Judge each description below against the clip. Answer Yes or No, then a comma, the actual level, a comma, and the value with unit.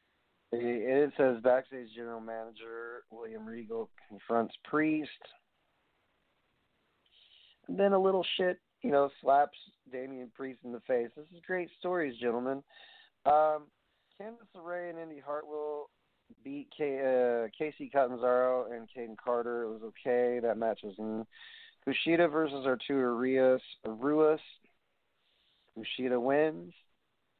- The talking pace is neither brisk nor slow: No, slow, 120 wpm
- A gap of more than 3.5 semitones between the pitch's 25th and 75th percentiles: Yes, average, 4.7 semitones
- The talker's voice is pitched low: Yes, low, 130 Hz